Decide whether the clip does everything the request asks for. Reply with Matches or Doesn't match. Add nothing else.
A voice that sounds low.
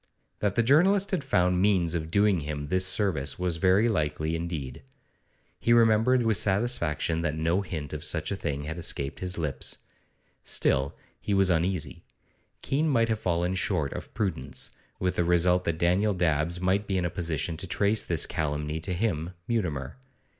Matches